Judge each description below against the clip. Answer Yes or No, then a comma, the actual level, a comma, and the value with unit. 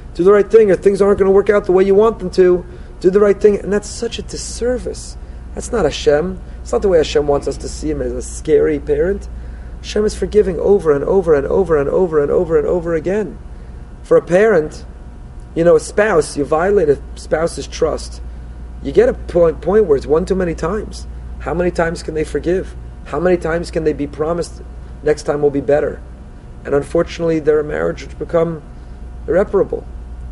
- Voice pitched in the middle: Yes, medium, 170 Hz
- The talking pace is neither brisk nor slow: No, fast, 210 wpm